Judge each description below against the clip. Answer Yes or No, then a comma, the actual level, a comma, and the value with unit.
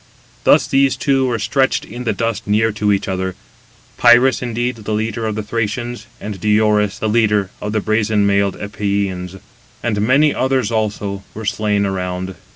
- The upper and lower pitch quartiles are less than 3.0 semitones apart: Yes, narrow, 2.6 semitones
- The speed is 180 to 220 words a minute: No, average, 165 wpm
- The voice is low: Yes, low, 110 Hz